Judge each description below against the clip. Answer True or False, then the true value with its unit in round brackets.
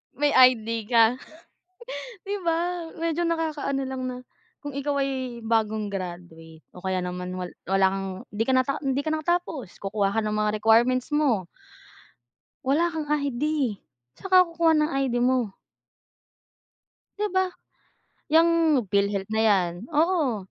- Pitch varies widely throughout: True (6.5 semitones)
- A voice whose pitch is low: False (255 Hz)